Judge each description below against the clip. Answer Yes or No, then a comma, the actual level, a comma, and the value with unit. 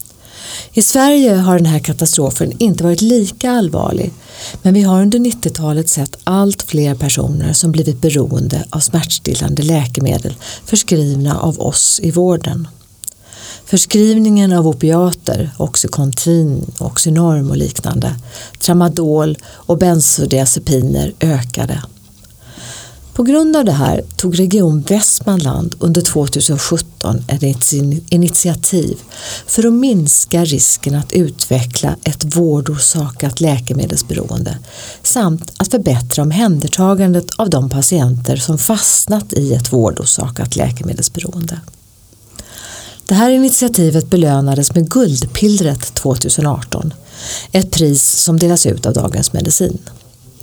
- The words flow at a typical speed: No, slow, 105 wpm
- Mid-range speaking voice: Yes, medium, 155 Hz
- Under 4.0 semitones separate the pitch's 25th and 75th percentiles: No, average, 5.0 semitones